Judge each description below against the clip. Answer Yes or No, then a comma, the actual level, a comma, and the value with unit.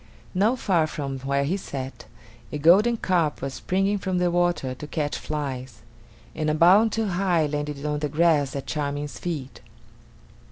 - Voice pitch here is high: No, medium, 155 Hz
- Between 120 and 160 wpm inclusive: No, average, 170 wpm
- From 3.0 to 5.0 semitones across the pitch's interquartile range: Yes, average, 4.2 semitones